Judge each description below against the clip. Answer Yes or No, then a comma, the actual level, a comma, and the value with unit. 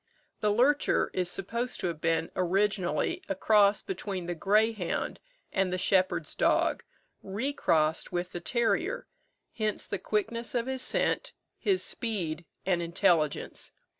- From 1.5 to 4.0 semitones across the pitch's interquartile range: No, average, 4.4 semitones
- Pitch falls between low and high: No, high, 195 Hz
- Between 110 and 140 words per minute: Yes, slow, 135 wpm